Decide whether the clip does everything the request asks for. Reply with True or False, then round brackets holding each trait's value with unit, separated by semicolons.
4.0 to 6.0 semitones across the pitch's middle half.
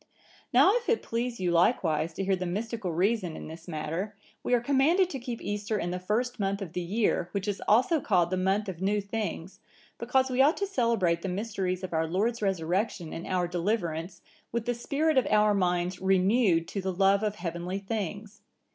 True (4.4 semitones)